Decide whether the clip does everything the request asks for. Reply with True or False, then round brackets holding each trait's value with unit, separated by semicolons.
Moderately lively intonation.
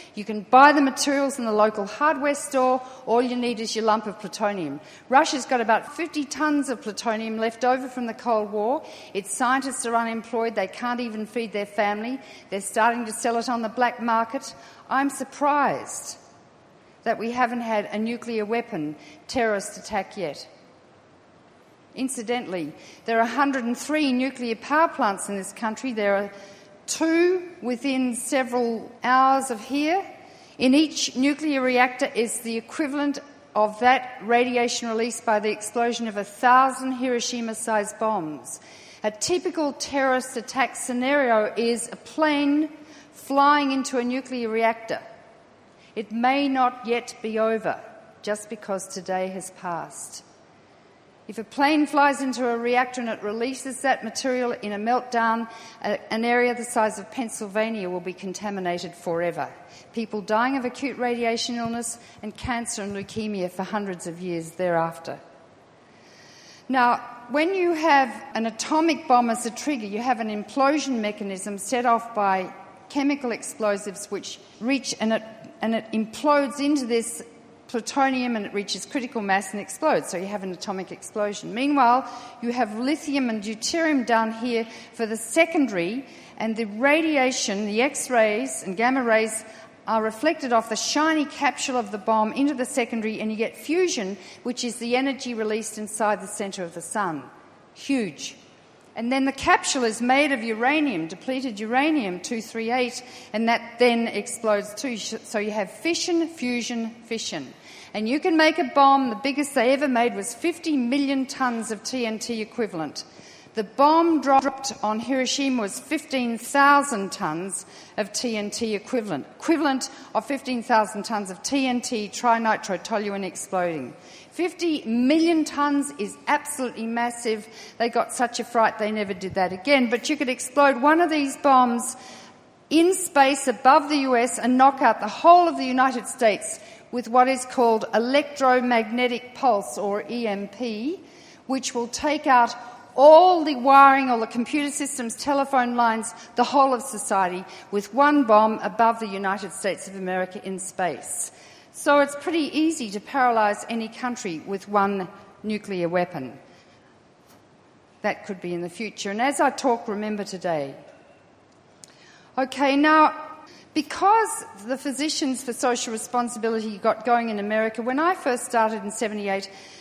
True (4.0 semitones)